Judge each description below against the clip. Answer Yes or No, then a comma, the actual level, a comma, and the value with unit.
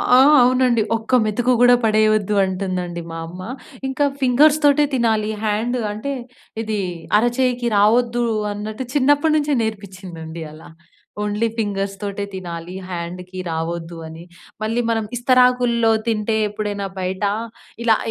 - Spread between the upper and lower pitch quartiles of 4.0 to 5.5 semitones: Yes, average, 4.4 semitones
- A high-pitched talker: Yes, high, 215 Hz